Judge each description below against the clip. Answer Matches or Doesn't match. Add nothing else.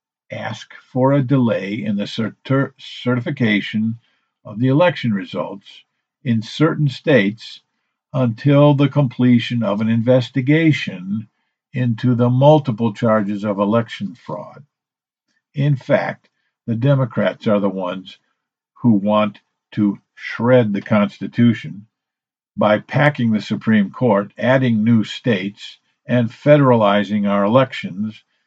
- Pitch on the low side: Matches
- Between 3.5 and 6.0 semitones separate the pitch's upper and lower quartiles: Matches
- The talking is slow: Matches